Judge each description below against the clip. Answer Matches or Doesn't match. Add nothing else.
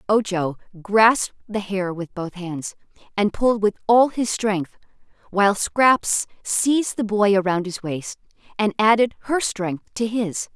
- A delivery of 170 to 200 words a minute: Doesn't match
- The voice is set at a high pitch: Matches